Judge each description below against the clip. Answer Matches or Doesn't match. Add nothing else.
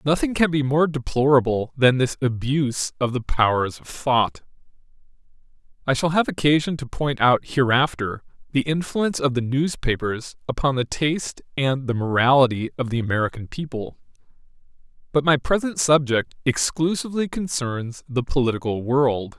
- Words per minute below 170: Matches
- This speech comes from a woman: Doesn't match